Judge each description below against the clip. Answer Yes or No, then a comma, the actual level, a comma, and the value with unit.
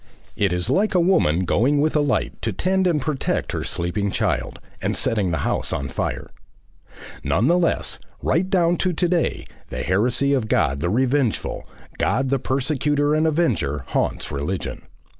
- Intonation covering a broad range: Yes, wide, 8.7 semitones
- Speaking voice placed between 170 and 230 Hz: No, low, 135 Hz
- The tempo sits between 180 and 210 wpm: No, average, 170 wpm